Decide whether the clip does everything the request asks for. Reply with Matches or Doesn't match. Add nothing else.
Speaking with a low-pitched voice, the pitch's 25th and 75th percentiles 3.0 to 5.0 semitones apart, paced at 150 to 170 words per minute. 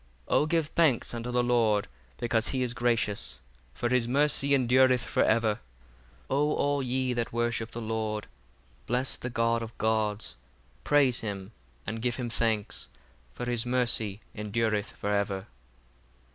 Doesn't match